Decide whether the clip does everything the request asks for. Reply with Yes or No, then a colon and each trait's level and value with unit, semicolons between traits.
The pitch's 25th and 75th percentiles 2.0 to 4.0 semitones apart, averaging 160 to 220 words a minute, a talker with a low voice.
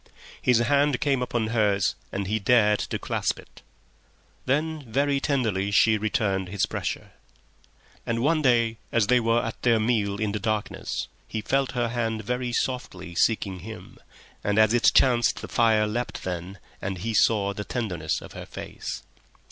Yes: average, 3.3 semitones; average, 165 wpm; low, 110 Hz